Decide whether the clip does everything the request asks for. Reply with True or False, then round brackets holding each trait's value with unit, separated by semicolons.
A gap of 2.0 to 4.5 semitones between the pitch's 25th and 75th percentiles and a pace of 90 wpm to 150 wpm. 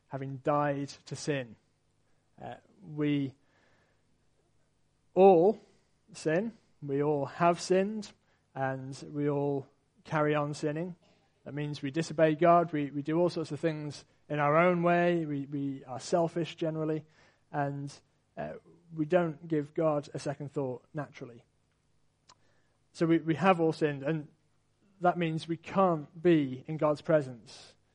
True (2.9 semitones; 135 wpm)